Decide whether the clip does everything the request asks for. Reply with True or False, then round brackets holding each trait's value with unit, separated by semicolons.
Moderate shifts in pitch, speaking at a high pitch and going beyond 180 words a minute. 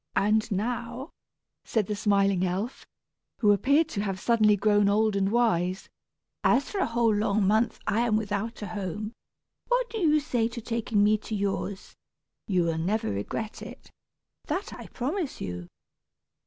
False (3.0 semitones; 215 Hz; 160 wpm)